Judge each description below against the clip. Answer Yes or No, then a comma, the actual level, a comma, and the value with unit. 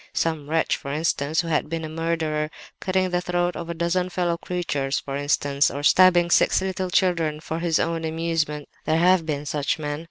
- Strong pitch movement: No, narrow, 2.6 semitones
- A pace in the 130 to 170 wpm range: No, average, 190 wpm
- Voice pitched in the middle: Yes, medium, 165 Hz